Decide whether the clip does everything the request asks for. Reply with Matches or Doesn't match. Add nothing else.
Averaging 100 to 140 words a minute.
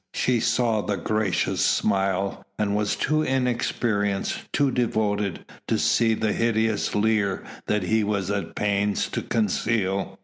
Matches